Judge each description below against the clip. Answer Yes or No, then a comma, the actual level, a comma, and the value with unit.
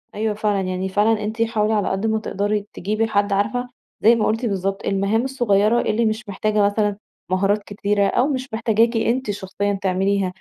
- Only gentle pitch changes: Yes, narrow, 1.9 semitones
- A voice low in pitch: No, high, 210 Hz